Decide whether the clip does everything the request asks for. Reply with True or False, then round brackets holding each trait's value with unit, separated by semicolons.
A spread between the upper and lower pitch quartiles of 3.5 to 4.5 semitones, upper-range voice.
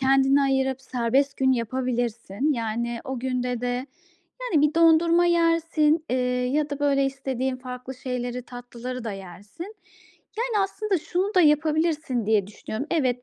True (4.0 semitones; 265 Hz)